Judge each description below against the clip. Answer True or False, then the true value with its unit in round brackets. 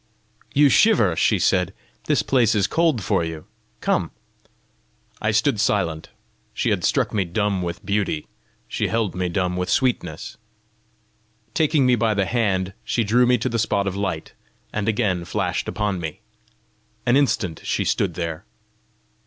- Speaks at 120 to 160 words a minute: True (155 wpm)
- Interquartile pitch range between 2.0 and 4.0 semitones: False (4.6 semitones)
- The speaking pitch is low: True (100 Hz)